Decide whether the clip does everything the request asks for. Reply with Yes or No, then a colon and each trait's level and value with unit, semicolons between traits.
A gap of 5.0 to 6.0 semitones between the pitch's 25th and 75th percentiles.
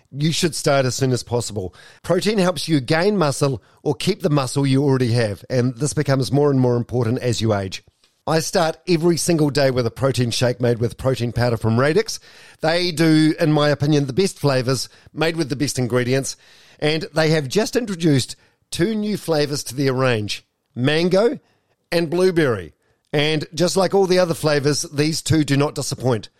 No: average, 4.6 semitones